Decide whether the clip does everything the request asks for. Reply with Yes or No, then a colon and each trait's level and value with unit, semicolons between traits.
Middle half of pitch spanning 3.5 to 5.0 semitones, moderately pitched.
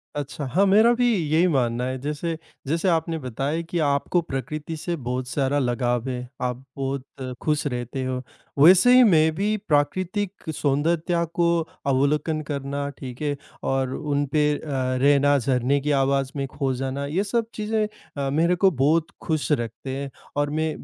Yes: average, 3.8 semitones; medium, 145 Hz